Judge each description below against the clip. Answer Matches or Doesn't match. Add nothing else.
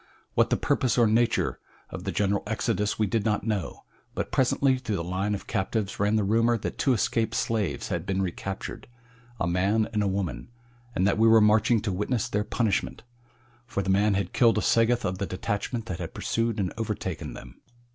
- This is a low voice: Matches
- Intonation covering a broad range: Doesn't match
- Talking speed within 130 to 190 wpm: Doesn't match